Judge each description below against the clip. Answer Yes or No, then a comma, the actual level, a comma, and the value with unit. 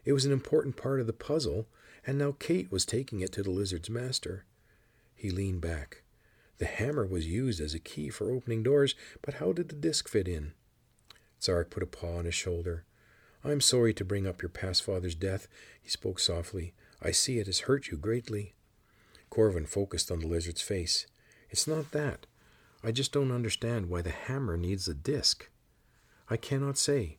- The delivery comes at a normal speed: Yes, average, 190 wpm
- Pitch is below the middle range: Yes, low, 110 Hz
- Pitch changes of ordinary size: No, wide, 6.4 semitones